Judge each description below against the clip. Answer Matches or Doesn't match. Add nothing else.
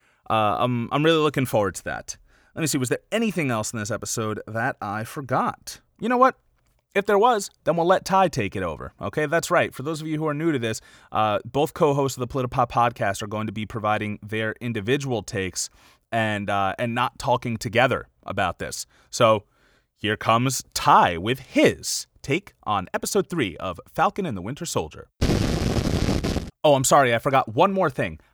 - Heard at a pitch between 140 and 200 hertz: Doesn't match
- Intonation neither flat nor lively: Doesn't match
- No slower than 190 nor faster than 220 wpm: Matches